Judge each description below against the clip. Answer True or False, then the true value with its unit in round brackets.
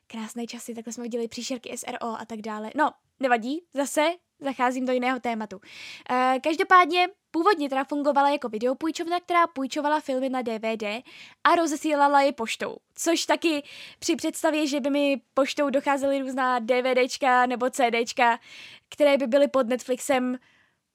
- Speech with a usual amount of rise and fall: True (3.5 semitones)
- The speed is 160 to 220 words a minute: False (145 wpm)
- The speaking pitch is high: True (270 Hz)